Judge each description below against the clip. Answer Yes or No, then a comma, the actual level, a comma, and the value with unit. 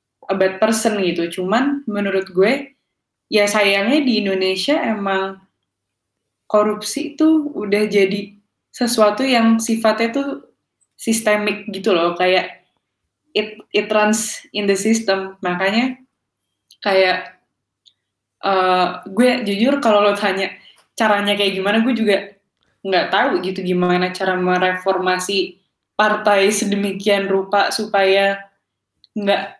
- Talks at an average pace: Yes, average, 110 wpm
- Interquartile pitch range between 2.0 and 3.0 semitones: Yes, narrow, 2.4 semitones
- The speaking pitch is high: Yes, high, 200 Hz